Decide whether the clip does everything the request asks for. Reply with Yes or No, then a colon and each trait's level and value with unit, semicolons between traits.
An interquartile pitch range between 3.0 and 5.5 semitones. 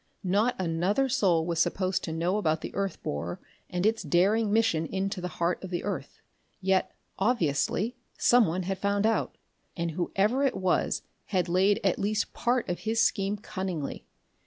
Yes: average, 3.4 semitones